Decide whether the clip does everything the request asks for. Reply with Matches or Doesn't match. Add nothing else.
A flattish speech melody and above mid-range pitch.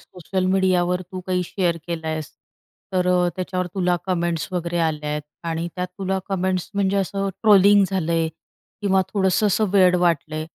Doesn't match